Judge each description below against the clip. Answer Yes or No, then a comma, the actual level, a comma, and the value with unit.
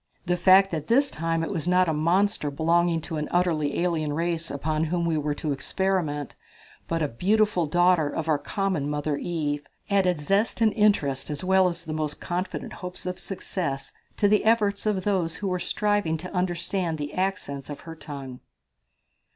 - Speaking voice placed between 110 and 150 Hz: No, medium, 170 Hz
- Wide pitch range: No, average, 3.8 semitones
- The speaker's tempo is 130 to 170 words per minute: No, average, 185 wpm